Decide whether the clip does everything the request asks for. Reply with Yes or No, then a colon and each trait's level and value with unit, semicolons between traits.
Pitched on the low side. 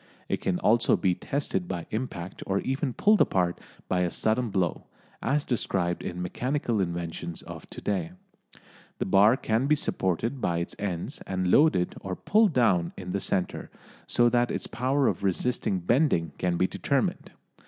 Yes: low, 100 Hz